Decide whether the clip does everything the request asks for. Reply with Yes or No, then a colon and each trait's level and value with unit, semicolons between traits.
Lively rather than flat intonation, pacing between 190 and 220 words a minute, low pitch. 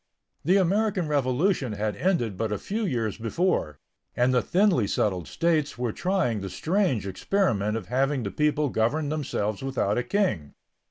No: wide, 8.5 semitones; average, 160 wpm; low, 130 Hz